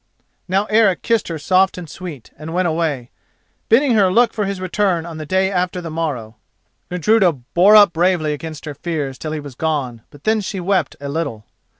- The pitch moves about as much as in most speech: Yes, average, 3.9 semitones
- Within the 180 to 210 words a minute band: Yes, average, 200 wpm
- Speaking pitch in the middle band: Yes, medium, 170 Hz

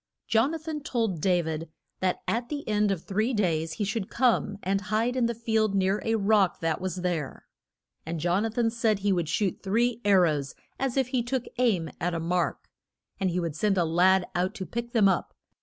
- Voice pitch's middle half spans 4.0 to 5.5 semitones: Yes, average, 4.5 semitones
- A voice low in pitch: No, high, 200 Hz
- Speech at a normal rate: No, fast, 225 wpm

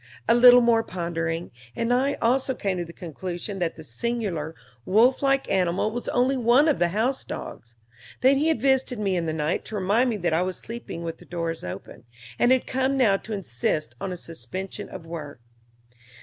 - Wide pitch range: Yes, wide, 6.5 semitones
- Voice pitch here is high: Yes, high, 195 Hz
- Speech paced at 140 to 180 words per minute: No, average, 200 wpm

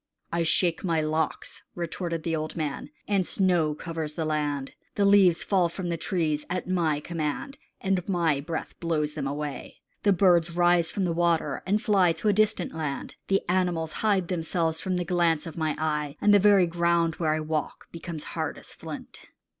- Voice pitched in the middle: Yes, medium, 170 Hz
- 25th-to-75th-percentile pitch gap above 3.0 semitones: No, narrow, 2.6 semitones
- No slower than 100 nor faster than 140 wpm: No, average, 190 wpm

